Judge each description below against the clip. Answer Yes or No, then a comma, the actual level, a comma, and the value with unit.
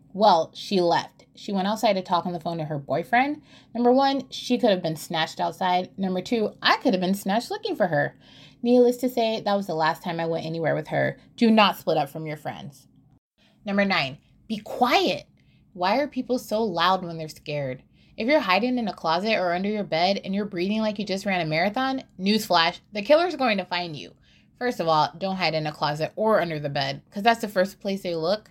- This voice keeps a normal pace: No, fast, 230 wpm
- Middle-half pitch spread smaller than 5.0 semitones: No, wide, 5.4 semitones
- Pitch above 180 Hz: Yes, high, 190 Hz